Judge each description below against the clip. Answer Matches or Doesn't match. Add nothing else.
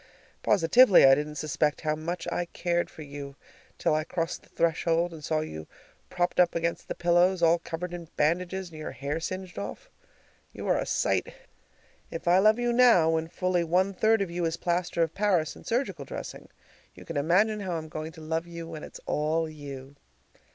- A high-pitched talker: Doesn't match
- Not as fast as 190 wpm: Doesn't match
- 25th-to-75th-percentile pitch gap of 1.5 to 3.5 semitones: Matches